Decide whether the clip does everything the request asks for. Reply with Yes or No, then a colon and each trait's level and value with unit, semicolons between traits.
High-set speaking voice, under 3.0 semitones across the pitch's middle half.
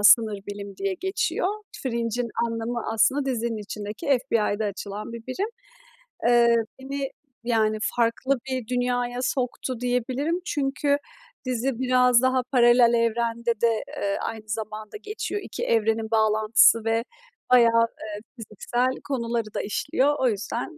Yes: high, 235 Hz; narrow, 2.6 semitones